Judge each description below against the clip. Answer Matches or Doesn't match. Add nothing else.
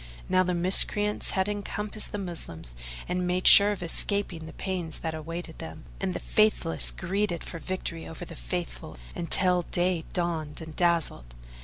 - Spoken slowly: Doesn't match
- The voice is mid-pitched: Matches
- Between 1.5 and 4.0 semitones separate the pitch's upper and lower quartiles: Matches